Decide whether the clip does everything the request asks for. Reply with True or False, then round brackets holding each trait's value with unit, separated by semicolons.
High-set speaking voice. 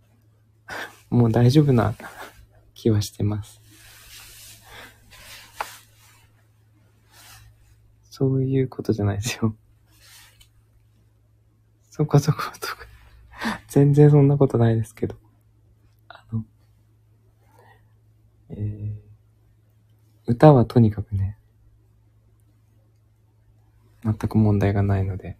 False (110 Hz)